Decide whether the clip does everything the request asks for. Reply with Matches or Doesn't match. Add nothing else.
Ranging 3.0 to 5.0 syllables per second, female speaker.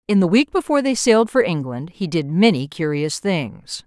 Doesn't match